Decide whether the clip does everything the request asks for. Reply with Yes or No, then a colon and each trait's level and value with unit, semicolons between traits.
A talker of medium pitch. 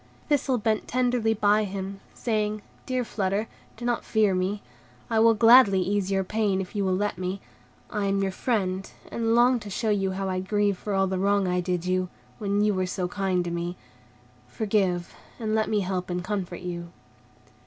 No: high, 200 Hz